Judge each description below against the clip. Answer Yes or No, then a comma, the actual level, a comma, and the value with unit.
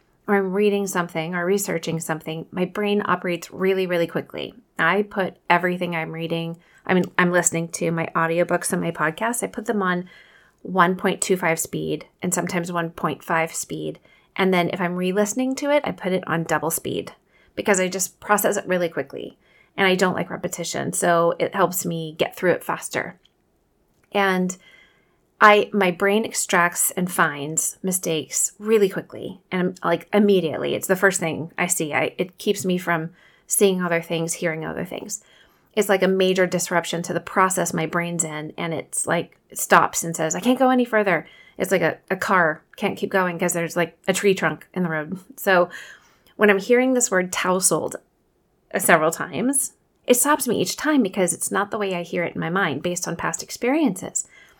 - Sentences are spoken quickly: No, average, 185 wpm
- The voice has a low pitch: No, medium, 180 Hz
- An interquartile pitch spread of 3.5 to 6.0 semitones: No, average, 2.8 semitones